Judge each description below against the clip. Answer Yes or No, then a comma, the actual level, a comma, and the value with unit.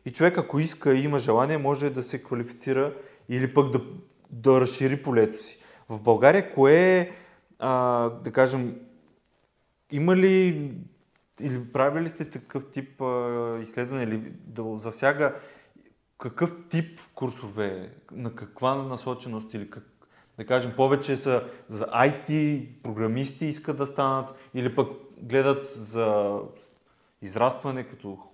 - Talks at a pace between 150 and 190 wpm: No, average, 130 wpm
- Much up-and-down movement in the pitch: No, average, 3.0 semitones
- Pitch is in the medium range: No, low, 130 Hz